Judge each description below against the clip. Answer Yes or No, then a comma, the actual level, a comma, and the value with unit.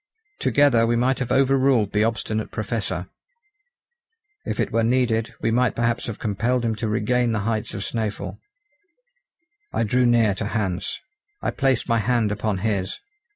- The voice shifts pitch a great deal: No, narrow, 2.6 semitones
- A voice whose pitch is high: No, low, 115 Hz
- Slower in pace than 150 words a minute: No, average, 160 wpm